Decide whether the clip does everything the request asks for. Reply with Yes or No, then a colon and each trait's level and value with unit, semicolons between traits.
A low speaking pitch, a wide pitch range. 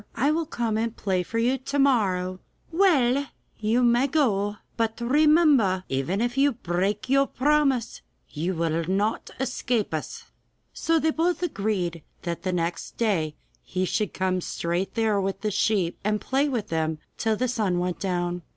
No: high, 215 Hz; wide, 6.2 semitones